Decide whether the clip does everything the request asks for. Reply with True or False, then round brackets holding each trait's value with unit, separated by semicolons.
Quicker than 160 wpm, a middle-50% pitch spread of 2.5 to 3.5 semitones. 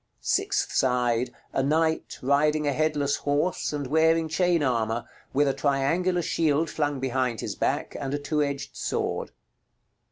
False (150 wpm; 2.9 semitones)